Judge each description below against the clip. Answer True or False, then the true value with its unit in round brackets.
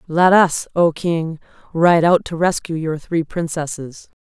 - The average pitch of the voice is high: False (165 Hz)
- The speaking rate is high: False (155 wpm)